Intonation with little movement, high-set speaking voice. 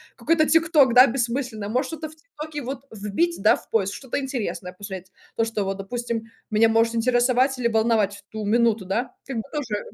No: average, 4.1 semitones; high, 235 Hz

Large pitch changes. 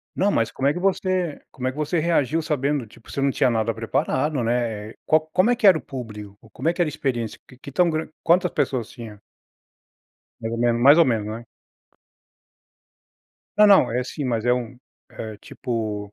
Yes: wide, 5.7 semitones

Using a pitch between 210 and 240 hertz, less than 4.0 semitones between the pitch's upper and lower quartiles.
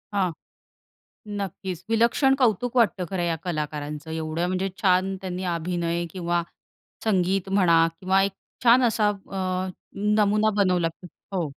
No: medium, 185 Hz; average, 2.8 semitones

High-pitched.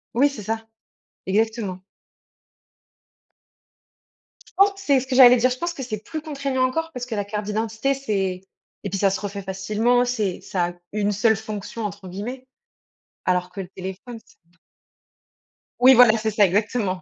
Yes: high, 220 Hz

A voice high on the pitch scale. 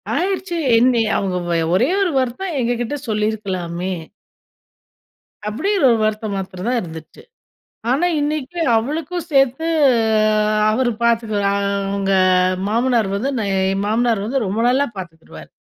Yes: high, 225 Hz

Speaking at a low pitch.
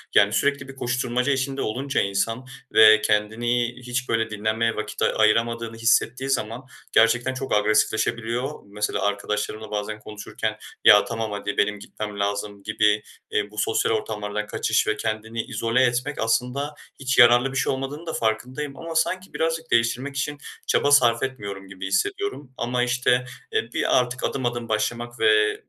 Yes: low, 115 Hz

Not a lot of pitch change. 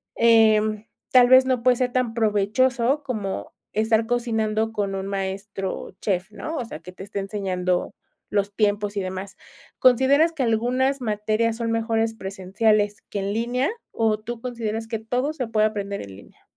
No: average, 3.2 semitones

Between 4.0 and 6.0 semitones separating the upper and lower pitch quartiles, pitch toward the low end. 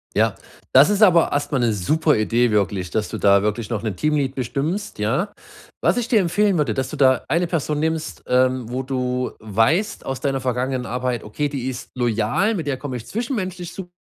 Yes: wide, 5.5 semitones; low, 130 Hz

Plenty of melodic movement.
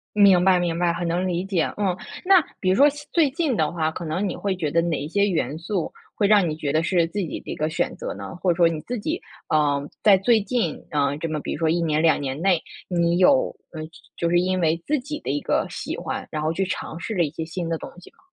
No: average, 3.5 semitones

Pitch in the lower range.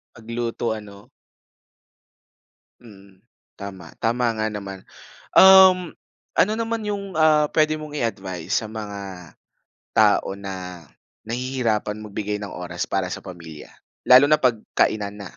Yes: low, 110 Hz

